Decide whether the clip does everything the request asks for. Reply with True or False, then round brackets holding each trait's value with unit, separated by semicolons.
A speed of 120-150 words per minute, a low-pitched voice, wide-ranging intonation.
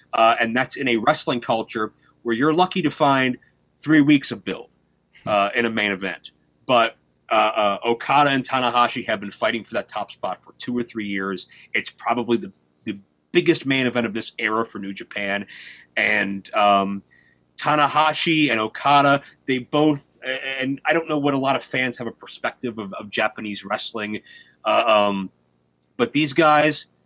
False (175 wpm; 115 Hz; 5.8 semitones)